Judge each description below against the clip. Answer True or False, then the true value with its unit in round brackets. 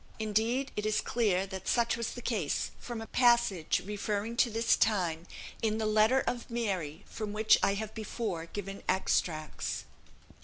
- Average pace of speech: True (160 wpm)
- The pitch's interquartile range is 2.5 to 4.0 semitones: True (3.1 semitones)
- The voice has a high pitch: True (215 Hz)